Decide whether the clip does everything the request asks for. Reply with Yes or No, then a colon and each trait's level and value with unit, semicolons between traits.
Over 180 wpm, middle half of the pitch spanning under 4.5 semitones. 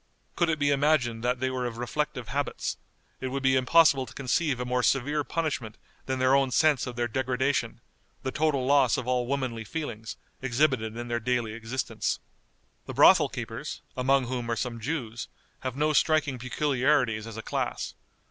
No: average, 175 wpm; average, 2.8 semitones